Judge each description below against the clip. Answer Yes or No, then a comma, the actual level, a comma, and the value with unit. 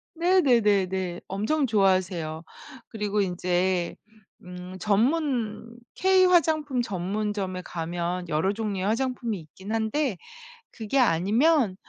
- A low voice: No, high, 205 Hz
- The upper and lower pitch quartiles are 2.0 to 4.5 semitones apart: No, wide, 5.4 semitones